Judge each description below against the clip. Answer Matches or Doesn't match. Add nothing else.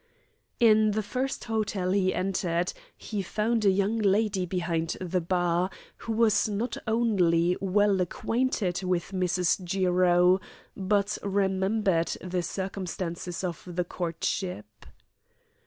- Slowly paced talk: Matches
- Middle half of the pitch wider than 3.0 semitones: Doesn't match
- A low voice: Doesn't match